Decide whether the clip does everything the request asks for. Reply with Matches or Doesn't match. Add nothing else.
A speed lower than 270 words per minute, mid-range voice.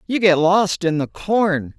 Matches